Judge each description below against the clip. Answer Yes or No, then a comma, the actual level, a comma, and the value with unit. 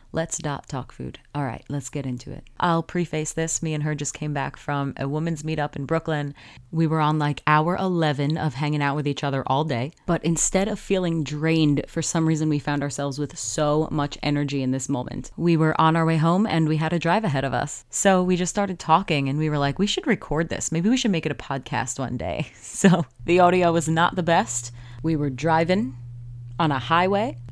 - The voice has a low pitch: No, medium, 155 Hz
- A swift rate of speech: Yes, fast, 230 wpm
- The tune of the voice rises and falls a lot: No, average, 2.8 semitones